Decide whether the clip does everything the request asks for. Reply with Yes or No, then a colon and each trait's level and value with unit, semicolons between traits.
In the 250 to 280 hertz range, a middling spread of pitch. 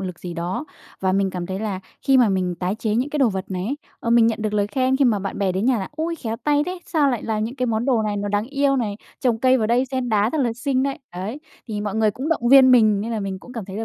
No: high, 225 Hz; average, 4.4 semitones